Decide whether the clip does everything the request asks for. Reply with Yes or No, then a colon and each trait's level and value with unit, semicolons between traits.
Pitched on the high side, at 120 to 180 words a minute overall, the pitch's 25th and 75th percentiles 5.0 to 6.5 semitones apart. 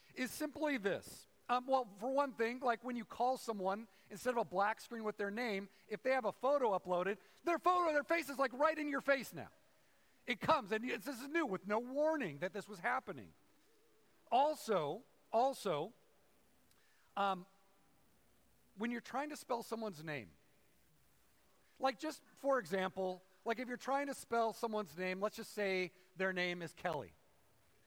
Yes: high, 230 Hz; average, 175 wpm; wide, 5.5 semitones